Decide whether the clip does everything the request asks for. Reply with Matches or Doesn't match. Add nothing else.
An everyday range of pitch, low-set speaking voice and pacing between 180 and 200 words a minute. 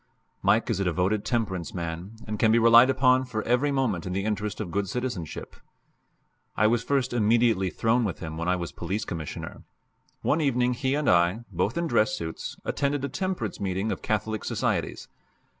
Matches